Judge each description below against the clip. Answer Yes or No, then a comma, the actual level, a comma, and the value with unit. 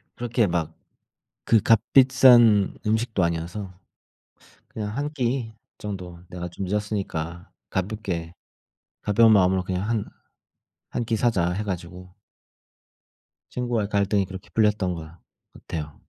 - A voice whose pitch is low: Yes, low, 100 Hz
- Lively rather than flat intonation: No, average, 4.0 semitones